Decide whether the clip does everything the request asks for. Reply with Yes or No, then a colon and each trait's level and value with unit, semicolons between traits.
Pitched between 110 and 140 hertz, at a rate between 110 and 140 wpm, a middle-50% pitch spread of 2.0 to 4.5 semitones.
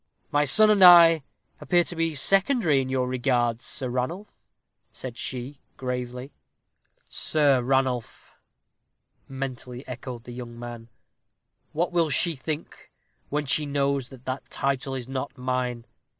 Yes: low, 135 Hz; slow, 135 wpm; average, 3.2 semitones